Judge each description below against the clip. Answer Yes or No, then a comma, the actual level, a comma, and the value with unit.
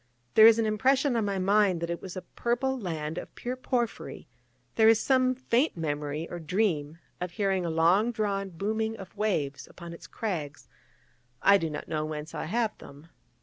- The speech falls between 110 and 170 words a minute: No, average, 190 wpm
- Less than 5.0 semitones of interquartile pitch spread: No, average, 5.3 semitones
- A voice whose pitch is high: Yes, high, 195 Hz